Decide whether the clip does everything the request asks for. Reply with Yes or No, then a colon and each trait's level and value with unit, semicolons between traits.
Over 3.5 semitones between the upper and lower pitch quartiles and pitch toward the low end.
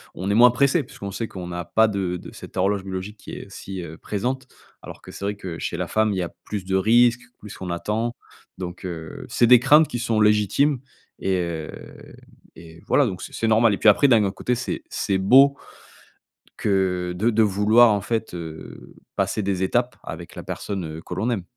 Yes: average, 4.0 semitones; low, 100 Hz